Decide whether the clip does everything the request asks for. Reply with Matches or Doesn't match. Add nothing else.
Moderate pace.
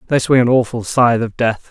Doesn't match